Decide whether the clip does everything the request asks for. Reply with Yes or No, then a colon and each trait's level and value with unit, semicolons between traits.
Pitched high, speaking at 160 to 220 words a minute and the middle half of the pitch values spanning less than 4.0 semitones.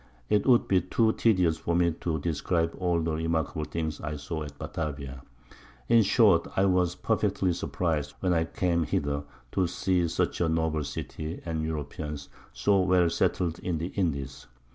No: very low, 85 Hz; average, 165 wpm; average, 3.0 semitones